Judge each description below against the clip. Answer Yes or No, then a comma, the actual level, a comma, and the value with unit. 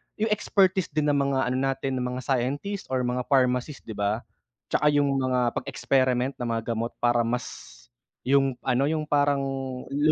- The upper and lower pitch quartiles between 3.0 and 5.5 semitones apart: No, narrow, 2.5 semitones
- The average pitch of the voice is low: Yes, low, 130 Hz